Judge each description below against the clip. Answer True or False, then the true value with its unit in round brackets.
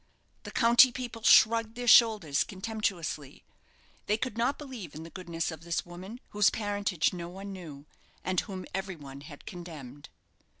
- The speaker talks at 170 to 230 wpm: False (160 wpm)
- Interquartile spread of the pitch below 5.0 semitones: False (5.3 semitones)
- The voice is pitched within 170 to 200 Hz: True (190 Hz)